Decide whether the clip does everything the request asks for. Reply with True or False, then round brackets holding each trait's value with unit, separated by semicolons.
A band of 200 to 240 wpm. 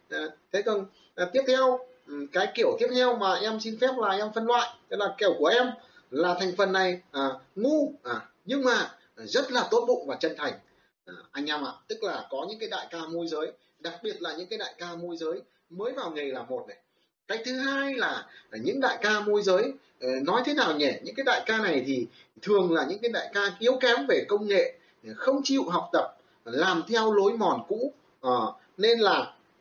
True (220 wpm)